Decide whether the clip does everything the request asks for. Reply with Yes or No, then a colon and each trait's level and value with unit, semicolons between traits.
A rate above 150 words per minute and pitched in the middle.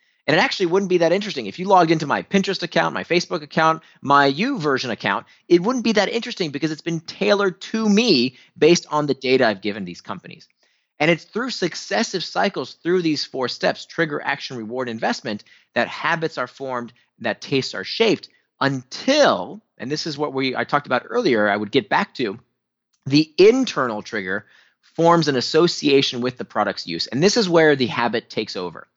Yes: average, 180 wpm; medium, 160 Hz